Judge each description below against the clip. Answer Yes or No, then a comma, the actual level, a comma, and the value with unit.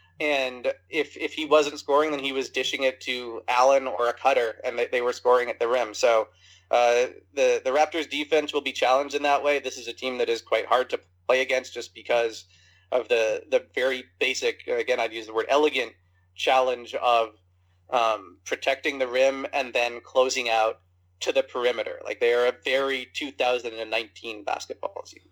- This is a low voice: Yes, low, 130 Hz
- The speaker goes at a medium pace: Yes, average, 190 wpm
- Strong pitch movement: Yes, wide, 5.9 semitones